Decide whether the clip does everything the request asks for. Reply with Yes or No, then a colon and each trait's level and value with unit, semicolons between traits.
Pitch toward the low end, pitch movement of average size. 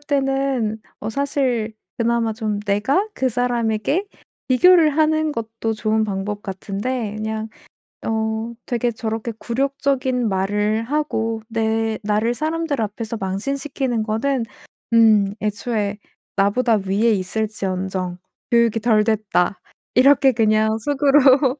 No: high, 225 Hz; average, 3.6 semitones